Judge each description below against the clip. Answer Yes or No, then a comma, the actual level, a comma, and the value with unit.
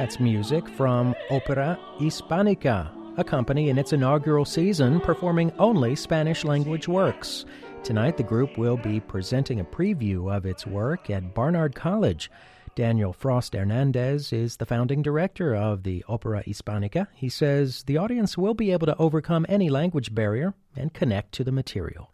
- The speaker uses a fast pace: No, average, 155 wpm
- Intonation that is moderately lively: No, wide, 6.4 semitones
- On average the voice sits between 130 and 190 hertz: Yes, low, 135 Hz